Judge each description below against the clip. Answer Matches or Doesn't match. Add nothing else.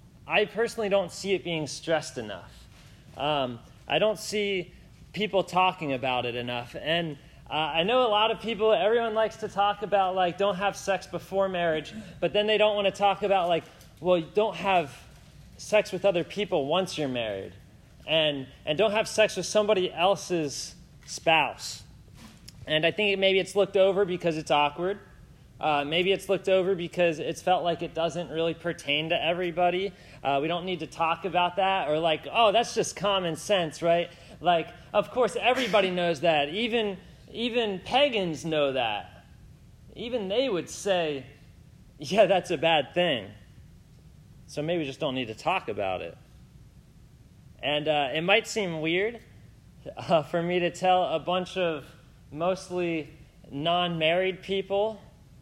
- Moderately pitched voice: Matches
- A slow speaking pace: Doesn't match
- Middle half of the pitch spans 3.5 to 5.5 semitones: Matches